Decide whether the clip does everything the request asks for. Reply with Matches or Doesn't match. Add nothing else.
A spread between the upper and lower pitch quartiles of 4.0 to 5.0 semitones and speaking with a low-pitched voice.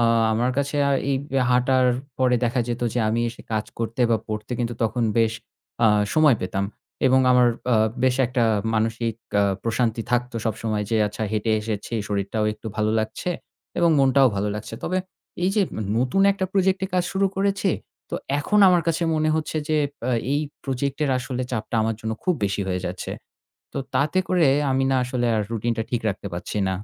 Matches